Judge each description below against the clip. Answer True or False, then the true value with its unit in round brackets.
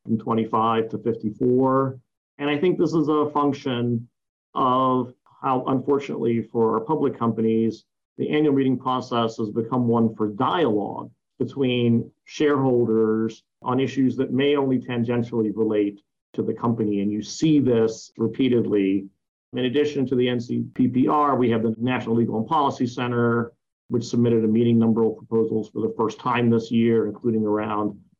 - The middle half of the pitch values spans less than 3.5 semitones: True (2.6 semitones)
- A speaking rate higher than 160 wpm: False (155 wpm)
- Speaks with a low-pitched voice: True (120 Hz)